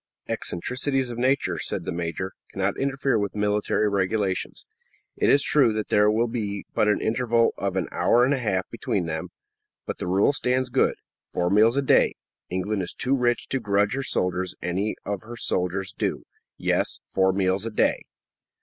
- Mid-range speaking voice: No, low, 105 Hz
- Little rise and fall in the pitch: No, average, 4.5 semitones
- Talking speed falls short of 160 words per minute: No, average, 180 wpm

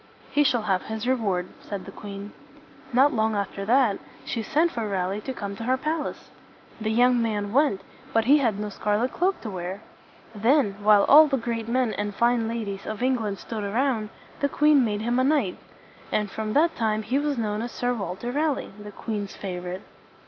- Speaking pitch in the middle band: No, high, 225 Hz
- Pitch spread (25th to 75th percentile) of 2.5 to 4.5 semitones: Yes, average, 4.0 semitones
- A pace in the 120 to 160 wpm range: No, average, 200 wpm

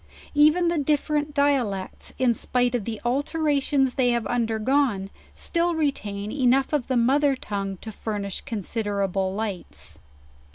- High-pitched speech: Yes, high, 245 Hz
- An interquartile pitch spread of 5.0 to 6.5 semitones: Yes, wide, 5.6 semitones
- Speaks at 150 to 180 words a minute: No, average, 140 wpm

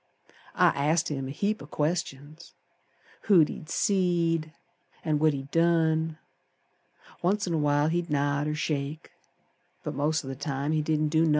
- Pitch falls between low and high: Yes, medium, 155 Hz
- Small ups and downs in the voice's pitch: Yes, narrow, 2.3 semitones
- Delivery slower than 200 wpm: Yes, average, 165 wpm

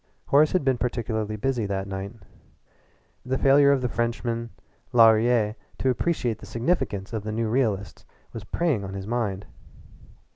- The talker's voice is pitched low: Yes, low, 115 Hz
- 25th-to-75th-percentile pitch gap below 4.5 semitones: Yes, average, 3.5 semitones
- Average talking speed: Yes, average, 150 wpm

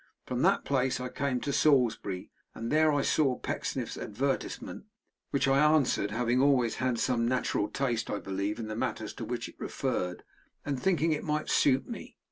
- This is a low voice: Yes, low, 130 Hz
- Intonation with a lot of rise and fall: No, average, 3.6 semitones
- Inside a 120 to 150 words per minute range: No, average, 180 wpm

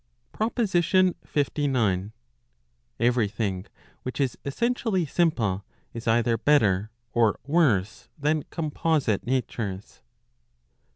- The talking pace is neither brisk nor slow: No, slow, 90 wpm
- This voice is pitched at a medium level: No, low, 130 Hz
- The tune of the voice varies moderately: No, wide, 6.7 semitones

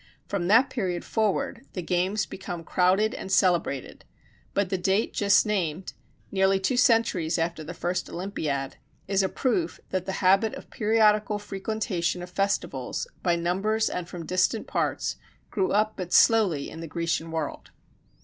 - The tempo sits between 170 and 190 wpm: No, average, 155 wpm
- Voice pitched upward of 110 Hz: Yes, high, 190 Hz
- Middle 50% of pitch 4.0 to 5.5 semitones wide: No, average, 3.3 semitones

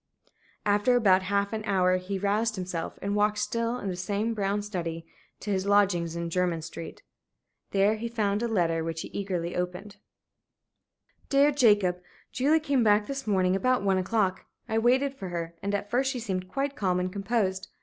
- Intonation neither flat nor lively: Yes, average, 3.5 semitones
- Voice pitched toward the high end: Yes, high, 200 Hz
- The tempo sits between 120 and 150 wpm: No, average, 180 wpm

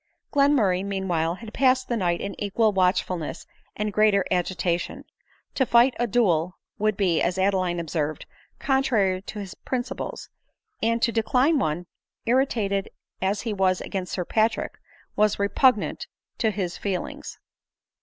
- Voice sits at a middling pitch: No, high, 200 Hz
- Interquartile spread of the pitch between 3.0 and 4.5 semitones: Yes, average, 4.2 semitones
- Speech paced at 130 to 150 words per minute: Yes, average, 140 wpm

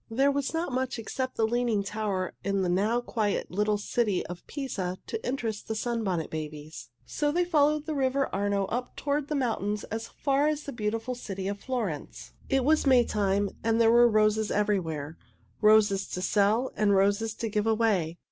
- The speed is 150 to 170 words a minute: No, average, 180 wpm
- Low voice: No, high, 220 Hz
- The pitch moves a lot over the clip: No, average, 4.4 semitones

